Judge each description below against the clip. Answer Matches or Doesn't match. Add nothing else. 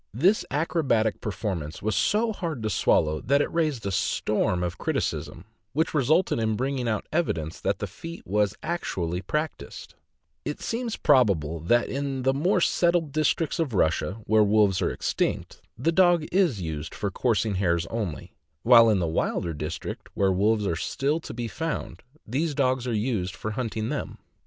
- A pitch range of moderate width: Doesn't match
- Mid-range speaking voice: Doesn't match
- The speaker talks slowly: Doesn't match